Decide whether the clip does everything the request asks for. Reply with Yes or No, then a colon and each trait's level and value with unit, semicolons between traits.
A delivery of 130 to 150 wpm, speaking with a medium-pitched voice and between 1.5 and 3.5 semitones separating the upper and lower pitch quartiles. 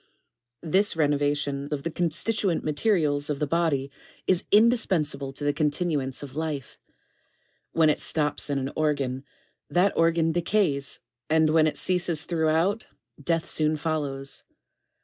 Yes: average, 140 wpm; medium, 155 Hz; average, 2.9 semitones